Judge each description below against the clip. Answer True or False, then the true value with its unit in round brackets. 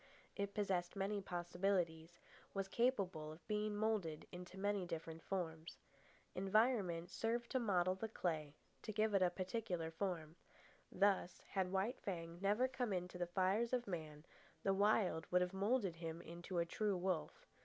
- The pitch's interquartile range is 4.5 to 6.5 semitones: False (3.2 semitones)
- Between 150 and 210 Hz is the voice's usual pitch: True (190 Hz)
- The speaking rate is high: False (160 wpm)